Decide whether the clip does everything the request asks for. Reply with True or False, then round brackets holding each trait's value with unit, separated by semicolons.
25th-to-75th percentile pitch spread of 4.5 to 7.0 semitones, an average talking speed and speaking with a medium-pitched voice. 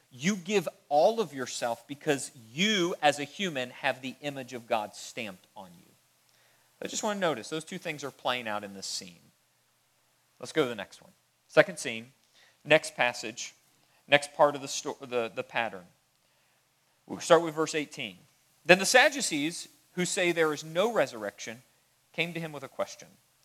True (5.1 semitones; 180 wpm; 145 Hz)